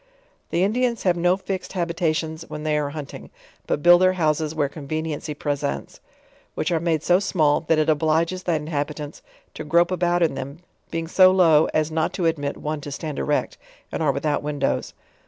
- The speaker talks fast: No, average, 190 wpm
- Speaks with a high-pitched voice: No, medium, 160 Hz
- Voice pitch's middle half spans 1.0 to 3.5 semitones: Yes, narrow, 2.6 semitones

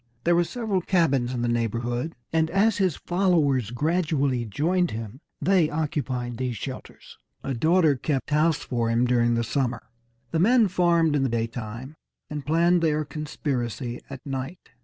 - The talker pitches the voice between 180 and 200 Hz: No, medium, 145 Hz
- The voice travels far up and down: Yes, wide, 5.7 semitones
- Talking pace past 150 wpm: Yes, average, 160 wpm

